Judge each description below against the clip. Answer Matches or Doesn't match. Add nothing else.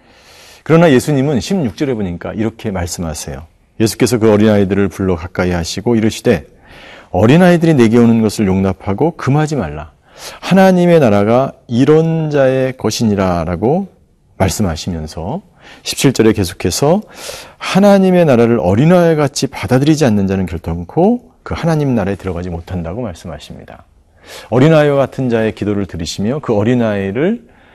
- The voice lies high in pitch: Doesn't match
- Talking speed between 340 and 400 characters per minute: Matches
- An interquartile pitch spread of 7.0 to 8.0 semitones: Matches